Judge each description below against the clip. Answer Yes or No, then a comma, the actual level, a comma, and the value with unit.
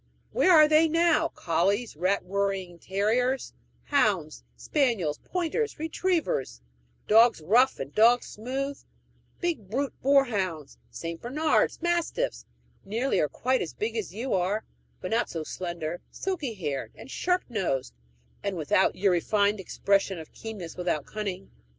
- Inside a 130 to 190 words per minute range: Yes, slow, 135 wpm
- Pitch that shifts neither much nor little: No, wide, 7.1 semitones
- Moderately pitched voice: No, high, 215 Hz